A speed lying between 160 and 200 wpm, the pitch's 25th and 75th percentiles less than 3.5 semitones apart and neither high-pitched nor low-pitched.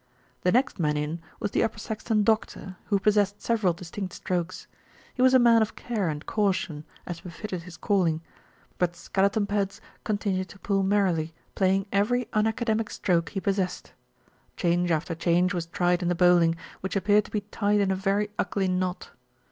No: average, 180 wpm; average, 2.8 semitones; high, 195 Hz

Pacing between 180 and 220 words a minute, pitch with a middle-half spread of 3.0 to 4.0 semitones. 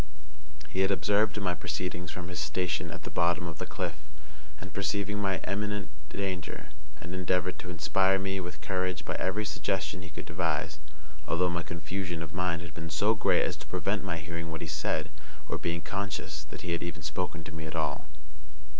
No: average, 195 wpm; narrow, 2.5 semitones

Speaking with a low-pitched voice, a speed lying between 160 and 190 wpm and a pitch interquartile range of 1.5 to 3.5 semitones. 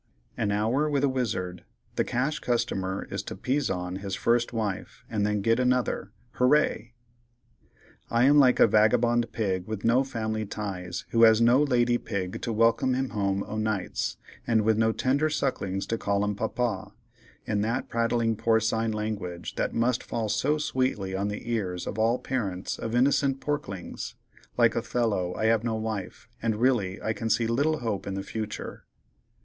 Yes: low, 110 Hz; average, 165 wpm; average, 3.2 semitones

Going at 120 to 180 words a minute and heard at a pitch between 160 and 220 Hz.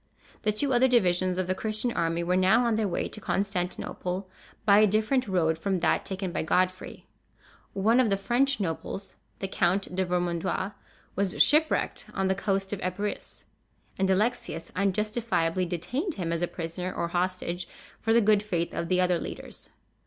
Yes: average, 175 wpm; high, 190 Hz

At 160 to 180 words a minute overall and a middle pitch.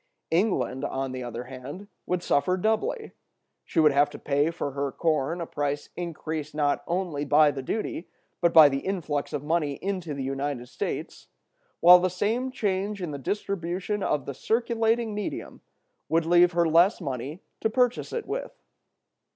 Yes: average, 165 wpm; medium, 165 Hz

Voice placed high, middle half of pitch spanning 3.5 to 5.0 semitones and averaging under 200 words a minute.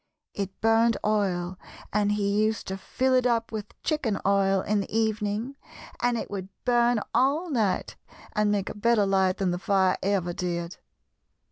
No: high, 210 Hz; average, 3.0 semitones; average, 165 wpm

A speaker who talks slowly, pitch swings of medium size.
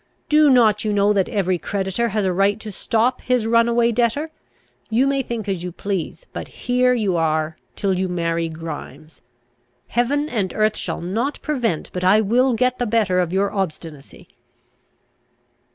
No: average, 170 wpm; average, 4.8 semitones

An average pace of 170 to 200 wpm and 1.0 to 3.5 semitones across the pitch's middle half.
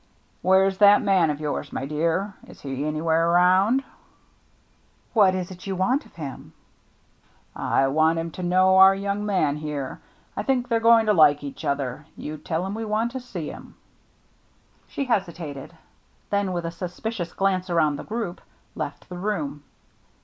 No: average, 180 wpm; average, 4.6 semitones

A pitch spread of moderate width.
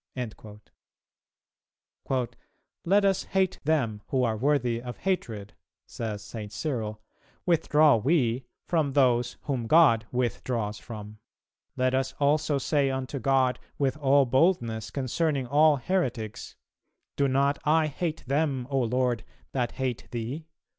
Yes: average, 4.1 semitones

